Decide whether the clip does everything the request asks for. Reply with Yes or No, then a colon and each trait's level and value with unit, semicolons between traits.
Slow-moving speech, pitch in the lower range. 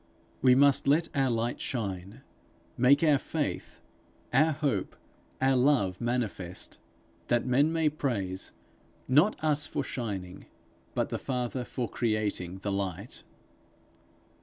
Yes: slow, 120 wpm; low, 125 Hz